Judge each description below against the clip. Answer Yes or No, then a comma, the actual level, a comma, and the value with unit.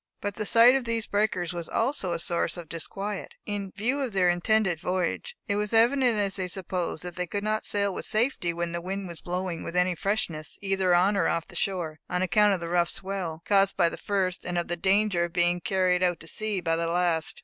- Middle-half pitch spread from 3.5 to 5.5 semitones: No, average, 3.0 semitones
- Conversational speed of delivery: No, fast, 235 wpm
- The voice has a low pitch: No, medium, 185 Hz